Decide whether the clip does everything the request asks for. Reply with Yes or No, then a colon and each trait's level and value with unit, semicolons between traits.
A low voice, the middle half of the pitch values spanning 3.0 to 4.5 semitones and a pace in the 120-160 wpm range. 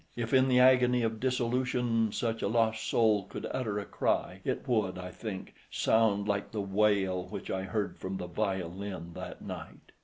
No: low, 110 Hz; average, 3.4 semitones; average, 180 wpm